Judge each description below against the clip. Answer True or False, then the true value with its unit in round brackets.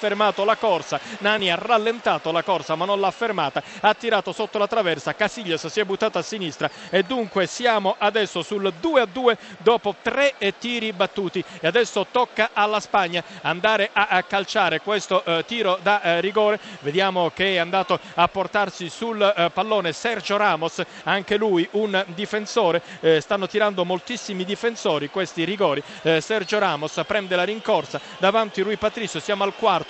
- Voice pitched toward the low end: False (200 Hz)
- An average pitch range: True (3.2 semitones)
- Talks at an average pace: True (155 wpm)